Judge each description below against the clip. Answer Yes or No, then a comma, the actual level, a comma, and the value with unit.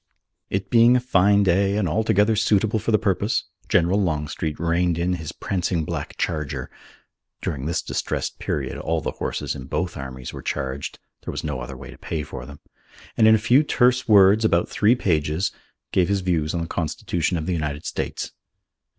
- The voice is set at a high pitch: No, very low, 90 Hz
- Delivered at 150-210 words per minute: Yes, average, 185 wpm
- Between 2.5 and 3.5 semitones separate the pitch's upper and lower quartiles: No, average, 5.1 semitones